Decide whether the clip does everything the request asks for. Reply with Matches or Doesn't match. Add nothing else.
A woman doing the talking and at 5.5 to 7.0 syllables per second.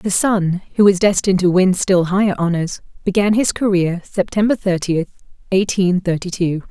Doesn't match